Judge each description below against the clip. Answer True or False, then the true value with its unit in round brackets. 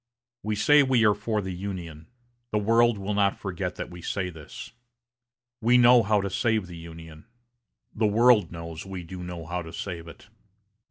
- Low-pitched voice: True (95 Hz)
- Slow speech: False (180 wpm)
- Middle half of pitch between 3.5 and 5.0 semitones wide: True (4.1 semitones)